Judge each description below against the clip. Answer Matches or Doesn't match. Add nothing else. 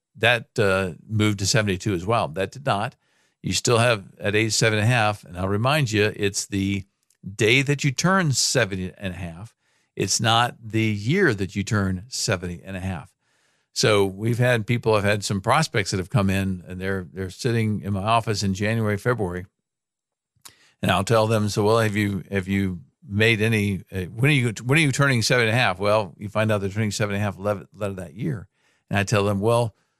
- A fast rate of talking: Matches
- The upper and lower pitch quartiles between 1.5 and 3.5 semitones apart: Matches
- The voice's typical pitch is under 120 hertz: Matches